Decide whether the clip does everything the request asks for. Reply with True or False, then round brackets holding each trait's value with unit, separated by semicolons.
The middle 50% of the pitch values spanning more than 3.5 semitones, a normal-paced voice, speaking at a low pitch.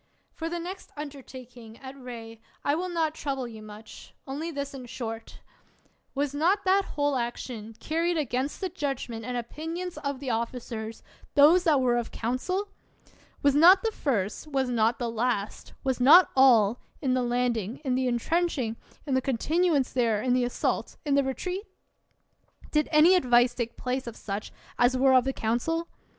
False (4.3 semitones; 170 wpm; 260 Hz)